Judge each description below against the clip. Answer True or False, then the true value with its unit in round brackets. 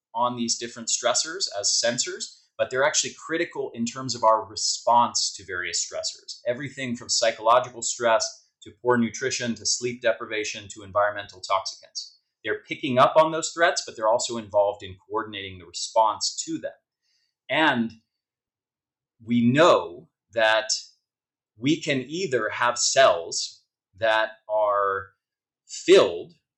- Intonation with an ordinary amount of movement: True (3.2 semitones)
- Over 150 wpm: False (135 wpm)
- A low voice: True (115 Hz)